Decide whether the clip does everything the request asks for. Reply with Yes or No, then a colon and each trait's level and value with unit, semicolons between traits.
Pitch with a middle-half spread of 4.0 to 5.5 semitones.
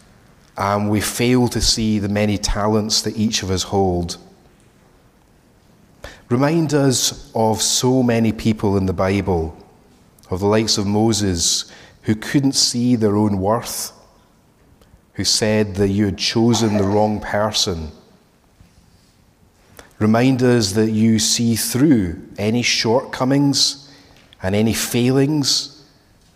No: average, 3.2 semitones